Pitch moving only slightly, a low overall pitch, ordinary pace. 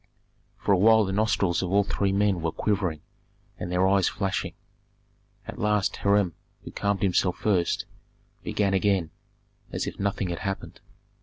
Yes: narrow, 2.0 semitones; very low, 95 Hz; average, 155 wpm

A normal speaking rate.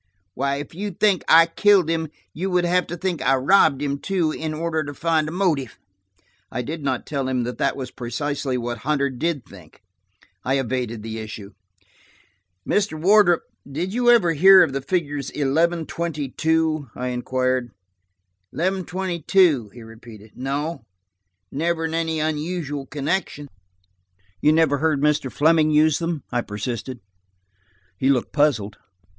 Yes: average, 155 wpm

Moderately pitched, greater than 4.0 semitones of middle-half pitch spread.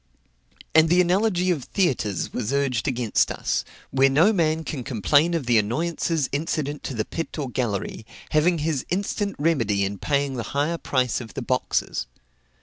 Yes: medium, 145 Hz; average, 5.2 semitones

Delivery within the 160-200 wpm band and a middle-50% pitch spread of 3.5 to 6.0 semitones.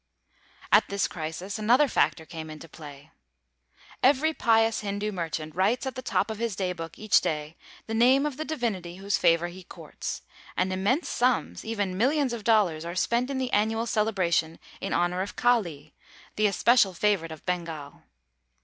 Yes: average, 170 wpm; wide, 5.6 semitones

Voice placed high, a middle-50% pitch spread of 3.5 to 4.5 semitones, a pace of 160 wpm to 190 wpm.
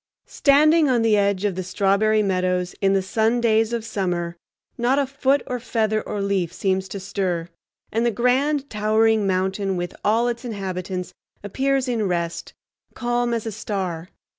Yes: high, 210 Hz; average, 4.1 semitones; average, 165 wpm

